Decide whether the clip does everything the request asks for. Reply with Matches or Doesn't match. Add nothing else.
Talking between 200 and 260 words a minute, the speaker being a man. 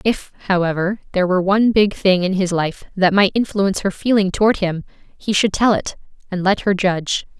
Doesn't match